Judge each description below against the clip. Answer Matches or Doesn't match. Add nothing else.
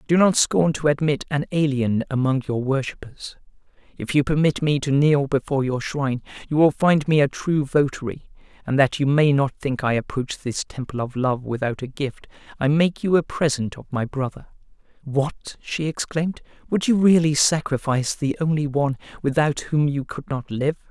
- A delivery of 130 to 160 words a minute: Doesn't match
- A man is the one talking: Matches